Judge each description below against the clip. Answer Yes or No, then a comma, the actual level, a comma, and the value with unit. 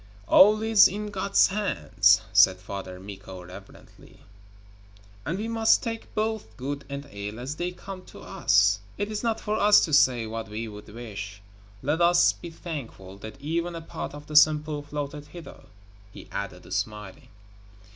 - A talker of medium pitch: Yes, medium, 145 Hz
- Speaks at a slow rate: No, average, 165 wpm